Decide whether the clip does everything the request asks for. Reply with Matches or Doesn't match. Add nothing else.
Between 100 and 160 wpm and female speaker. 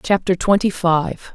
Matches